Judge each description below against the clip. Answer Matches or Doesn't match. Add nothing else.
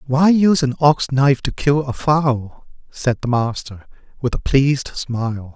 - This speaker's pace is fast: Doesn't match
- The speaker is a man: Matches